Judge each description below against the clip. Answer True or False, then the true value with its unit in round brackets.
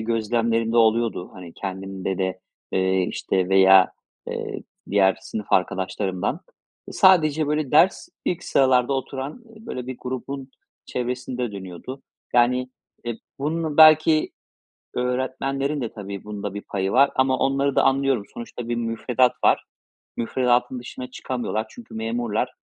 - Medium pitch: False (120 Hz)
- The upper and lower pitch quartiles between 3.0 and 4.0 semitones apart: False (4.7 semitones)